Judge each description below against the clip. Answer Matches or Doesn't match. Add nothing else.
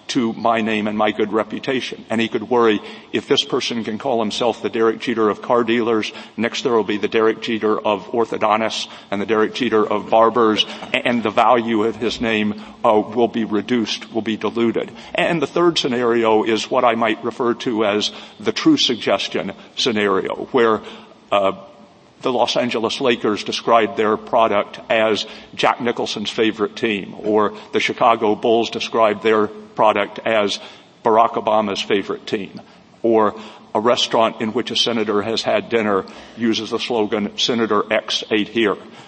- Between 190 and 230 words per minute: Doesn't match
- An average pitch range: Doesn't match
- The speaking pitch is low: Matches